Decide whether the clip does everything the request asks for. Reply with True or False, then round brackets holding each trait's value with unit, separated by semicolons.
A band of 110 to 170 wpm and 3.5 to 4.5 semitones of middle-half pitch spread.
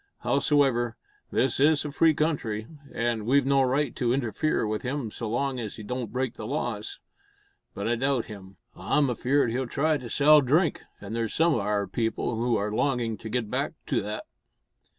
False (190 wpm; 4.0 semitones)